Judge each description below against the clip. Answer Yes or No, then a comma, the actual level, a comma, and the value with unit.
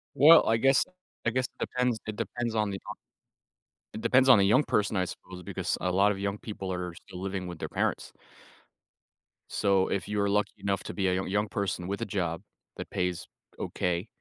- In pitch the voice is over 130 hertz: No, low, 100 Hz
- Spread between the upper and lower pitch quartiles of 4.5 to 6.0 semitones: No, average, 2.9 semitones